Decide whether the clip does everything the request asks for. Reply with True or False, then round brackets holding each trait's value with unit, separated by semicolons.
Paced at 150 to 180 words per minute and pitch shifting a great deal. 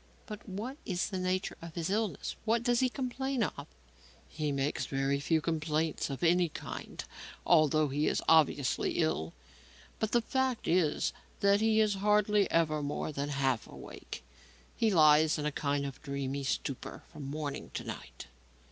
True (165 wpm; 6.4 semitones)